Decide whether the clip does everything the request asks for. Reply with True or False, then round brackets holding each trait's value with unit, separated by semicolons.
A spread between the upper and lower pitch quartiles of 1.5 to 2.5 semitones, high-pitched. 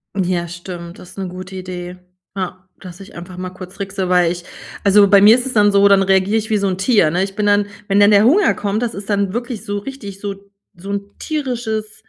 True (2.1 semitones; 200 Hz)